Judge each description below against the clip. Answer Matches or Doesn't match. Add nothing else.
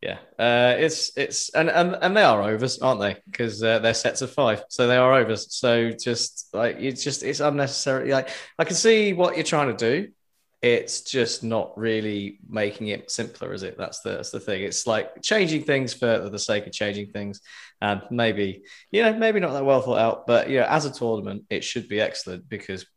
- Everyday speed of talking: Doesn't match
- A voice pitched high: Doesn't match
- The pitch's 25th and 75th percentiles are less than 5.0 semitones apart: Doesn't match